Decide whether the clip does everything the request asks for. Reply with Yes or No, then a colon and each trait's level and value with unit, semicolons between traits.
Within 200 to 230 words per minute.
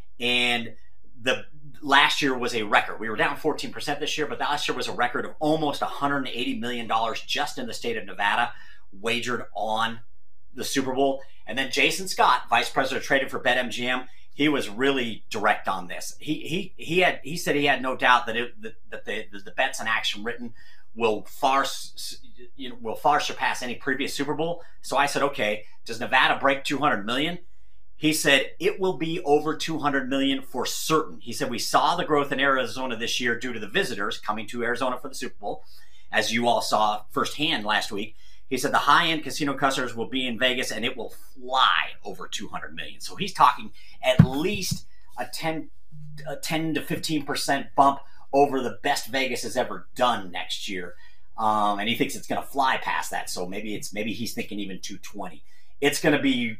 Yes: fast, 205 wpm